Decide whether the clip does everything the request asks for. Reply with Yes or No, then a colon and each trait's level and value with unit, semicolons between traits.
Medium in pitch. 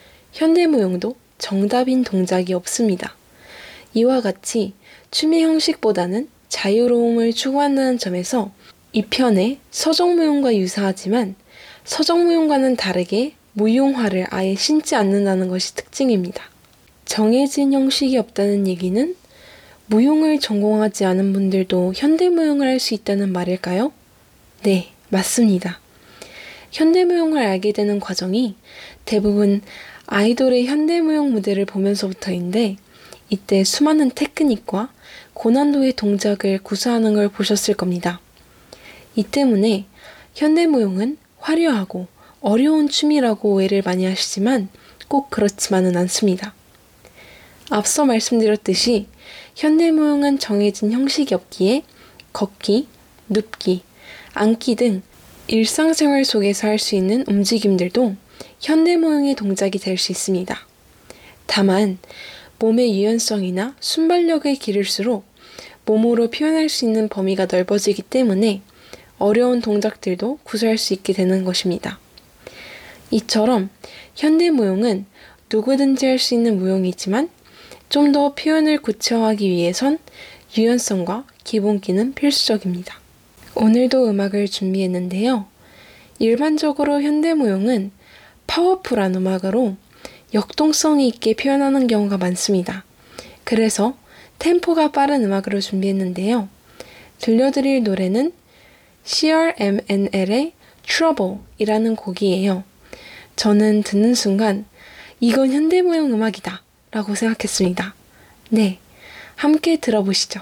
No: high, 220 Hz